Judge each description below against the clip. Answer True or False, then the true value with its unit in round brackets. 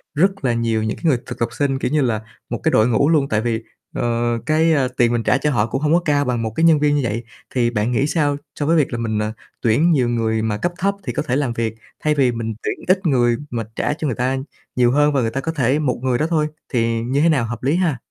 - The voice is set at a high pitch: False (130 Hz)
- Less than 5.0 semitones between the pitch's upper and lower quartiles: True (4.4 semitones)